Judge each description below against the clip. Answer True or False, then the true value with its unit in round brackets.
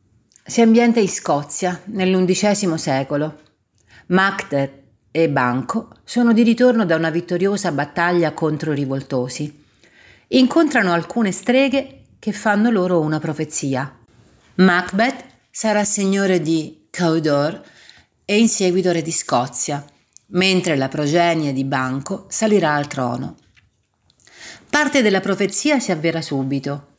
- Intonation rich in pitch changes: True (6.0 semitones)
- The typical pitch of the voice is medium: True (170 Hz)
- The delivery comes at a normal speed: False (110 wpm)